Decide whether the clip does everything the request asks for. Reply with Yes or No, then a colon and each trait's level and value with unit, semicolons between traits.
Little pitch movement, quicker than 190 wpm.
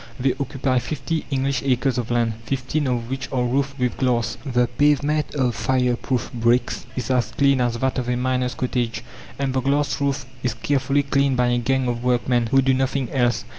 Yes: narrow, 2.0 semitones; average, 200 wpm